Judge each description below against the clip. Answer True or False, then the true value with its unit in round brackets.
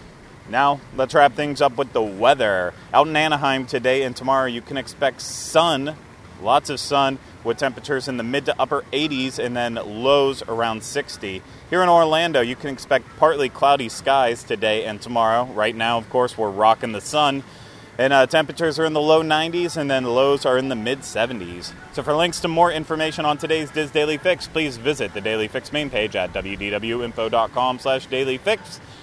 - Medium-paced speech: True (190 wpm)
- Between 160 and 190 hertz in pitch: False (135 Hz)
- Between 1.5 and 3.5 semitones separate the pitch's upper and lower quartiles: False (4.0 semitones)